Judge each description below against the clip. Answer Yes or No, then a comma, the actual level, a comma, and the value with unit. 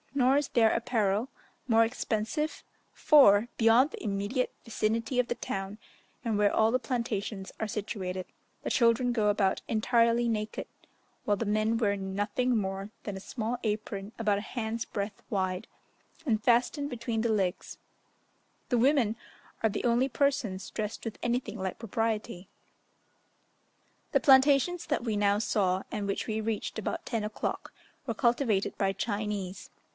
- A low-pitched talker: No, high, 220 Hz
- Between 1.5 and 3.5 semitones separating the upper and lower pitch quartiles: Yes, average, 2.9 semitones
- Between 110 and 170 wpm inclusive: Yes, average, 150 wpm